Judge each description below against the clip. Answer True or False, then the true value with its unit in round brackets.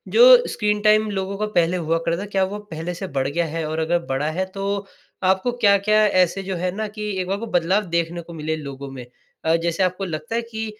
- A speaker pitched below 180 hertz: False (185 Hz)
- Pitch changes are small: False (3.6 semitones)